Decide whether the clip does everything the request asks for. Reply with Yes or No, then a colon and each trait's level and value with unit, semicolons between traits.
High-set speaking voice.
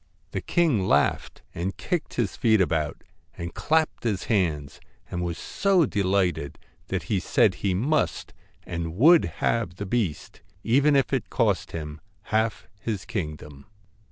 No: low, 100 Hz